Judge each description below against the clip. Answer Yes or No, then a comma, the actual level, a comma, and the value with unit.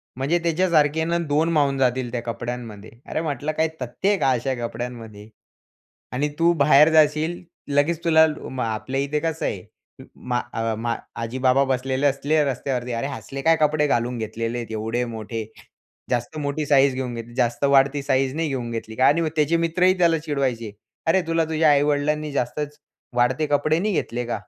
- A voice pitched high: No, medium, 140 Hz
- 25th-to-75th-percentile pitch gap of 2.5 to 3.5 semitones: No, average, 4.2 semitones